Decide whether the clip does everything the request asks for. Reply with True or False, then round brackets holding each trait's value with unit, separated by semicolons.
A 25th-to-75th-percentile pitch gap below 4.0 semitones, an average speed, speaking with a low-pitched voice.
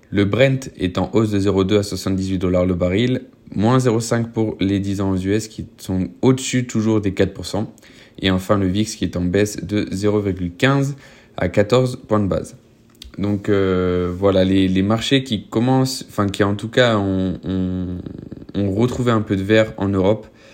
True (2.9 semitones; 185 wpm; 100 Hz)